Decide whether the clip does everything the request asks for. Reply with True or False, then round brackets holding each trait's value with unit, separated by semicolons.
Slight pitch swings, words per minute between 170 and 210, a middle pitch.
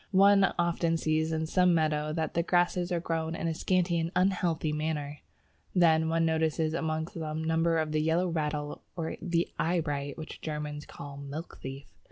True (1.7 semitones; 180 wpm; 160 Hz)